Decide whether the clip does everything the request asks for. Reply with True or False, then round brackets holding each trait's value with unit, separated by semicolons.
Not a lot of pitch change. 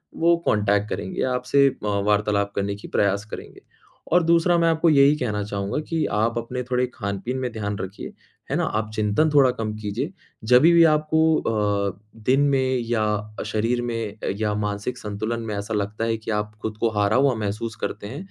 False (4.1 semitones)